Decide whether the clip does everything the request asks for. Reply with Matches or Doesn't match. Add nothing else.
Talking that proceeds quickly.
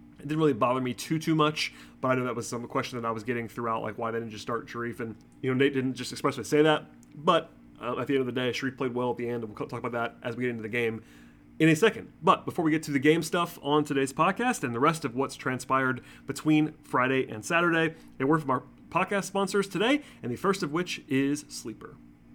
Matches